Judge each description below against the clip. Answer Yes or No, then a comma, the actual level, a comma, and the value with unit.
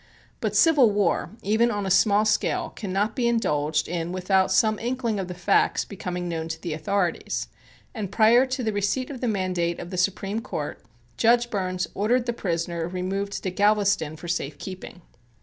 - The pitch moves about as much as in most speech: Yes, average, 3.7 semitones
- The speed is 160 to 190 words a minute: Yes, average, 180 wpm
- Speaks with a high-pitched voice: Yes, high, 195 Hz